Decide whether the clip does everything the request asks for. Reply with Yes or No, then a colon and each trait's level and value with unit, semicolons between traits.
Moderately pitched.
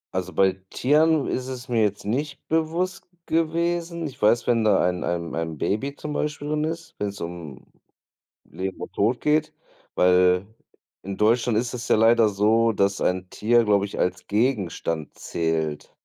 No: low, 110 Hz